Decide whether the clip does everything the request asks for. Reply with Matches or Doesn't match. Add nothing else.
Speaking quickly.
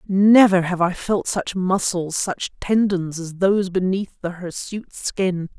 Doesn't match